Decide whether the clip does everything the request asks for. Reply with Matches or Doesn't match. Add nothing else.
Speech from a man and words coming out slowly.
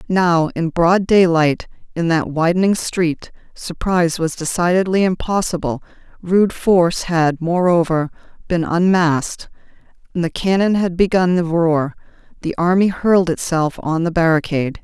Doesn't match